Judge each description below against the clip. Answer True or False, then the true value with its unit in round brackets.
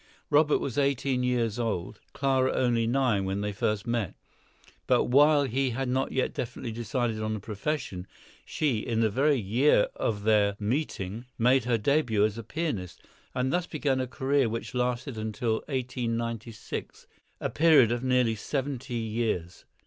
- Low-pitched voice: True (120 Hz)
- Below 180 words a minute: True (155 wpm)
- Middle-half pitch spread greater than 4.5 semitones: False (3.6 semitones)